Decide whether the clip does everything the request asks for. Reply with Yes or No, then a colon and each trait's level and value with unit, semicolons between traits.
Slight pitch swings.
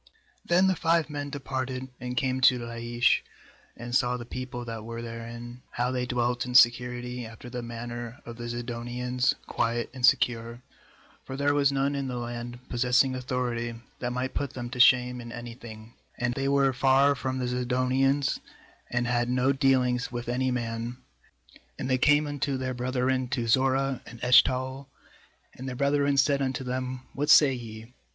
Yes: narrow, 1.7 semitones